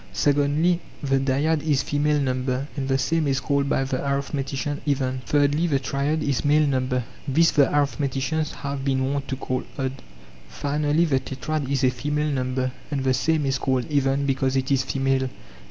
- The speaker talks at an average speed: Yes, average, 180 wpm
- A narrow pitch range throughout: Yes, narrow, 1.7 semitones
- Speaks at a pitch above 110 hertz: Yes, medium, 140 Hz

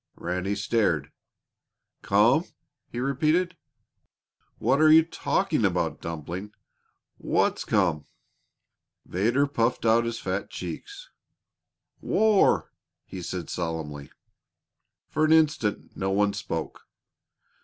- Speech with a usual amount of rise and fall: No, wide, 8.8 semitones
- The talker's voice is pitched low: Yes, low, 115 Hz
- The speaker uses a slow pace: Yes, slow, 100 wpm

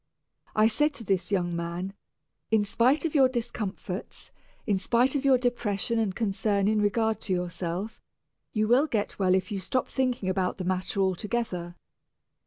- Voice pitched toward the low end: No, high, 205 Hz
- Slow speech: No, average, 170 wpm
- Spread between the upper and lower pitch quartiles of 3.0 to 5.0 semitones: Yes, average, 4.1 semitones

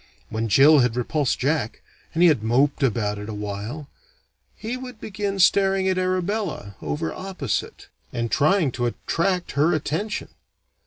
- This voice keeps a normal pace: Yes, average, 145 wpm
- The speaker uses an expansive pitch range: Yes, wide, 8.0 semitones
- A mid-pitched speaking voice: Yes, medium, 150 Hz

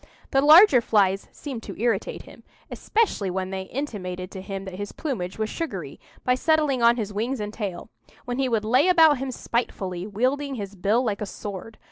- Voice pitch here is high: Yes, high, 220 Hz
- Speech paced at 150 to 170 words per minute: No, average, 190 wpm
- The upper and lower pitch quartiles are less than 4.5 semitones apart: No, average, 5.3 semitones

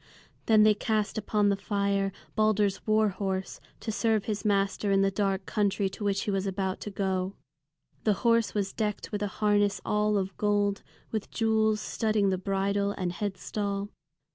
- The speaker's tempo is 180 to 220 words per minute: No, average, 170 wpm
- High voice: Yes, high, 205 Hz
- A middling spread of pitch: No, narrow, 1.4 semitones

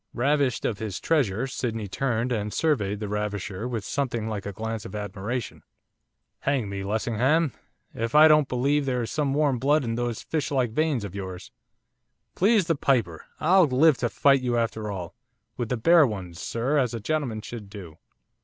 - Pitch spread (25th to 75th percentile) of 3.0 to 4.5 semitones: No, average, 5.1 semitones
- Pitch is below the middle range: Yes, low, 120 Hz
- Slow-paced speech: No, average, 180 wpm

